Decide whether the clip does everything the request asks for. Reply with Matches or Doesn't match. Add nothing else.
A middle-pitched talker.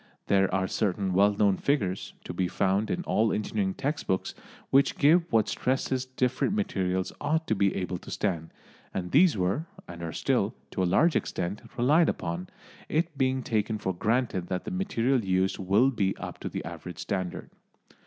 Doesn't match